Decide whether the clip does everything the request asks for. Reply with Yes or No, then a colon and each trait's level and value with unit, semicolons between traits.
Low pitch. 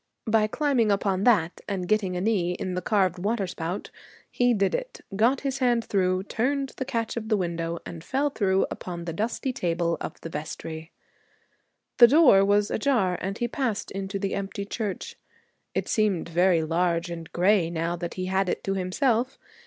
No: high, 195 Hz